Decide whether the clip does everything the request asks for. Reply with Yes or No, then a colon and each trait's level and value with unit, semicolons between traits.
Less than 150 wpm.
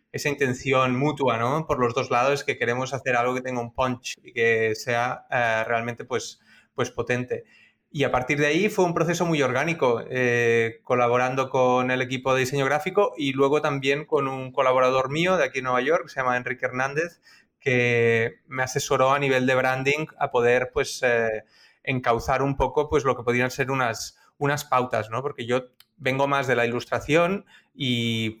No: fast, 190 wpm